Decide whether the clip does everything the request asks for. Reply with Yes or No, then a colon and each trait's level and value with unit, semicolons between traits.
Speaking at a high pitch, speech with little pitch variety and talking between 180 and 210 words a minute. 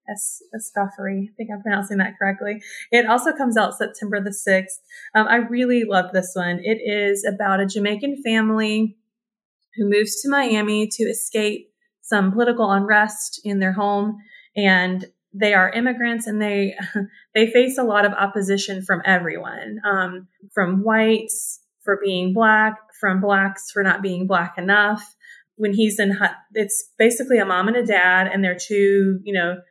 No: high, 205 Hz; narrow, 2.0 semitones; average, 165 wpm